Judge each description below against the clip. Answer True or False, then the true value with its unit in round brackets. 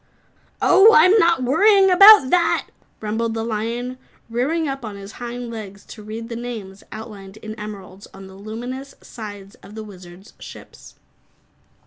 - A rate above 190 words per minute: False (150 wpm)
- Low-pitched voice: False (225 Hz)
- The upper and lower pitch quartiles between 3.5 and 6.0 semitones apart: True (4.0 semitones)